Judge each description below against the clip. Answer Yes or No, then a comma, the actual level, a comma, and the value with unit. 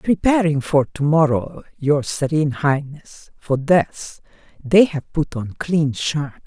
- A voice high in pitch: No, medium, 150 Hz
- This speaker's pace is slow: Yes, slow, 110 wpm